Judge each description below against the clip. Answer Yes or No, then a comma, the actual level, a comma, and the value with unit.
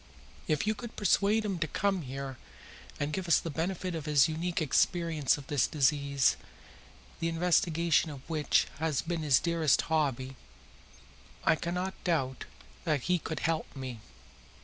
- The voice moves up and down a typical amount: Yes, average, 3.4 semitones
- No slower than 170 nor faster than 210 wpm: No, average, 150 wpm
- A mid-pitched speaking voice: Yes, medium, 160 Hz